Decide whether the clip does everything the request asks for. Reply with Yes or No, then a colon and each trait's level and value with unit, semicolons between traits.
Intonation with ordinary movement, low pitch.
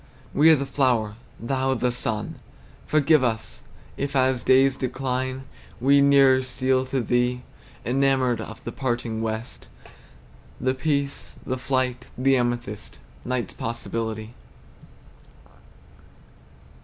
No: narrow, 2.0 semitones; low, 130 Hz